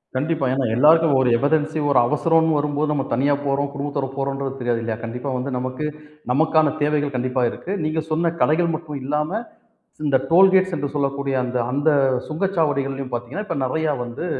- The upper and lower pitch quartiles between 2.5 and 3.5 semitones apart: Yes, average, 2.9 semitones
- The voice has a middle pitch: Yes, medium, 145 Hz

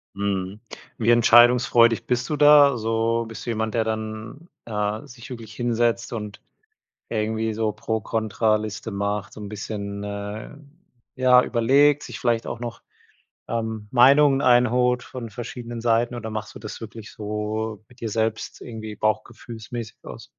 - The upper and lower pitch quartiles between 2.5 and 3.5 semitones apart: No, narrow, 2.0 semitones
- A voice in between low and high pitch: No, low, 115 Hz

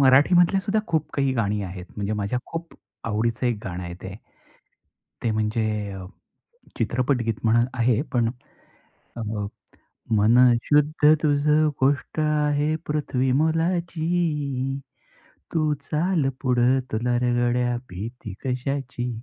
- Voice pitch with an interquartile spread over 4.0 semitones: Yes, average, 4.6 semitones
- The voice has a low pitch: Yes, low, 130 Hz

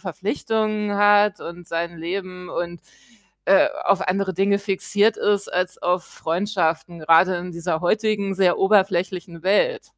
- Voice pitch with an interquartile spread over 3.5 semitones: No, average, 2.8 semitones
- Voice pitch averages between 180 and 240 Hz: Yes, high, 190 Hz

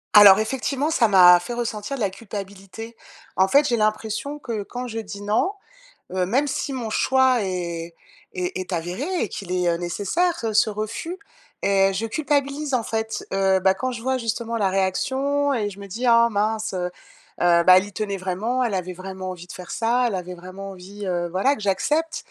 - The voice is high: Yes, high, 210 Hz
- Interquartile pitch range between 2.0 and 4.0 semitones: No, average, 4.6 semitones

